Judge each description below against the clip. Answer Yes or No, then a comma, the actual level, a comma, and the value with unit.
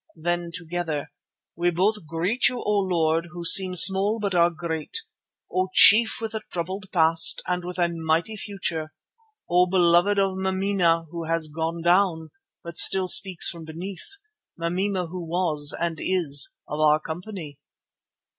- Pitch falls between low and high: Yes, medium, 175 Hz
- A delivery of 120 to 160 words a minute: Yes, average, 150 wpm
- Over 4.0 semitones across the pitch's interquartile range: No, narrow, 2.6 semitones